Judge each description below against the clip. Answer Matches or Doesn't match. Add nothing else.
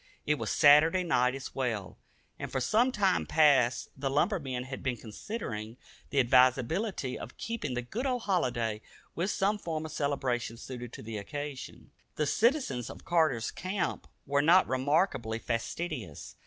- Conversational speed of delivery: Matches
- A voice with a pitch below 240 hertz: Matches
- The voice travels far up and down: Matches